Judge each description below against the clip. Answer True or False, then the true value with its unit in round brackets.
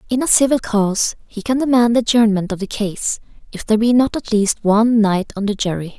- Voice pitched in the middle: False (220 Hz)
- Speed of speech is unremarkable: False (230 wpm)